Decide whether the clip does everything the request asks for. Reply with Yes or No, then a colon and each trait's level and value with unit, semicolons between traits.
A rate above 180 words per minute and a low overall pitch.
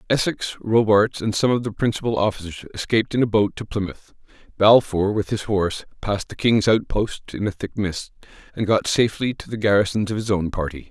Yes: average, 200 wpm; low, 105 Hz